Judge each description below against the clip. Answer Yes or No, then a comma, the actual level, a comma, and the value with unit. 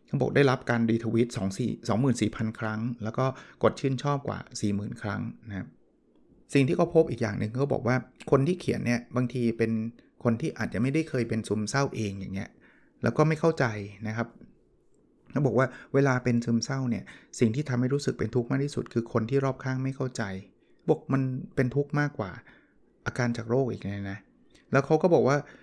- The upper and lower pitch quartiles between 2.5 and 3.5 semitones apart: Yes, average, 3.1 semitones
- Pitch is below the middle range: Yes, low, 120 Hz